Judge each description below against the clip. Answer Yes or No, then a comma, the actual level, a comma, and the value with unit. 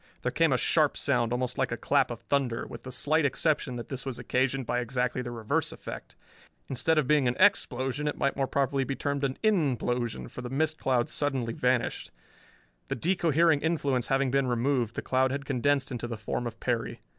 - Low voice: Yes, low, 130 Hz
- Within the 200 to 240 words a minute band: Yes, fast, 205 wpm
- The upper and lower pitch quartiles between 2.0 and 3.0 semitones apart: Yes, narrow, 2.6 semitones